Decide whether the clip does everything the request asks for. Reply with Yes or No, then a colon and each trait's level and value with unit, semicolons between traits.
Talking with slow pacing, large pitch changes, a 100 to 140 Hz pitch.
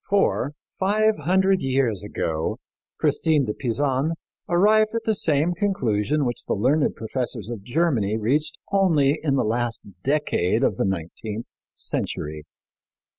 Yes: slow, 130 wpm; wide, 7.7 semitones; low, 135 Hz